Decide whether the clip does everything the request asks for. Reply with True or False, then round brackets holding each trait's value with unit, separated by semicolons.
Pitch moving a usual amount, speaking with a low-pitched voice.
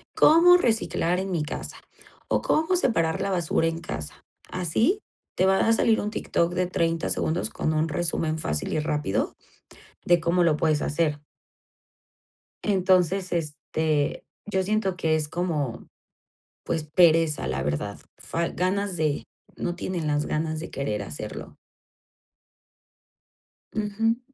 False (3.6 semitones; 170 Hz)